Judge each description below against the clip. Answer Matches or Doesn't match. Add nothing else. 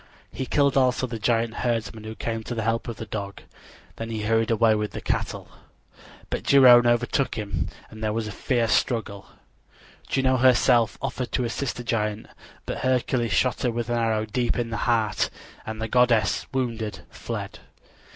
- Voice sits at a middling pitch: Doesn't match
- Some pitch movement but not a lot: Doesn't match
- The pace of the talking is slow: Doesn't match